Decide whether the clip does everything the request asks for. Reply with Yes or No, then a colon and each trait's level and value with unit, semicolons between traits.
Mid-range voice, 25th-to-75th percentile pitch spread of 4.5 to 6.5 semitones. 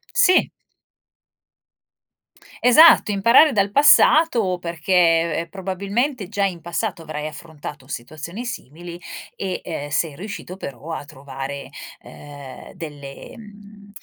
Yes: medium, 175 Hz; average, 5.2 semitones